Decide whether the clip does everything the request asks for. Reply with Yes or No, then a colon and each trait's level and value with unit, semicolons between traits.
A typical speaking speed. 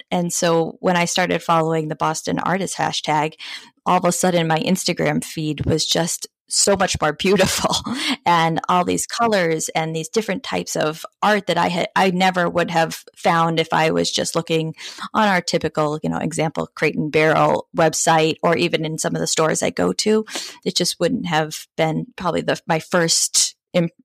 Yes: average, 190 wpm